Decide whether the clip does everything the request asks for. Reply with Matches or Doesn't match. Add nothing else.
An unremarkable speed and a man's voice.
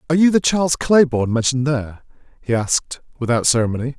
Matches